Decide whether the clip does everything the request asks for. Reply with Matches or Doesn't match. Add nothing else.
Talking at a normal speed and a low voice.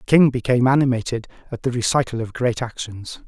Matches